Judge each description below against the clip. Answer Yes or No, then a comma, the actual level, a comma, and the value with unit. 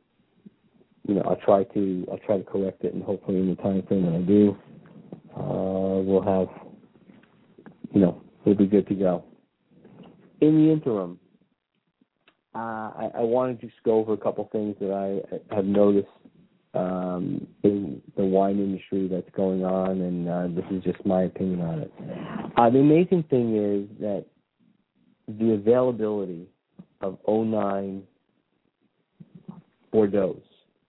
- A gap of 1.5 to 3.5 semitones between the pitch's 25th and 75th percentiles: Yes, narrow, 2.5 semitones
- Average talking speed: Yes, average, 150 wpm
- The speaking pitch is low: Yes, low, 100 Hz